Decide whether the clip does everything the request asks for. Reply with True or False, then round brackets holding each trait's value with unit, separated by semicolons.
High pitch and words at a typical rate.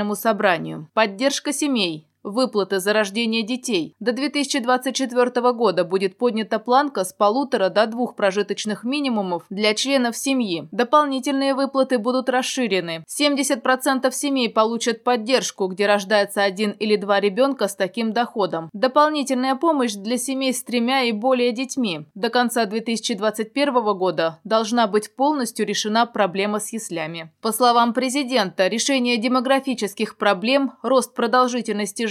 True (235 Hz; 125 wpm)